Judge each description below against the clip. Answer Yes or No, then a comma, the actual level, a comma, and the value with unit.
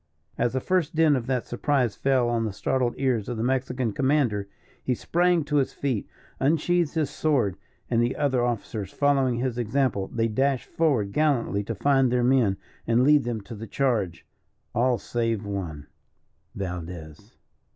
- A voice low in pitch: Yes, low, 125 Hz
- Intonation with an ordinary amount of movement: Yes, average, 3.9 semitones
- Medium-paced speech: Yes, average, 165 wpm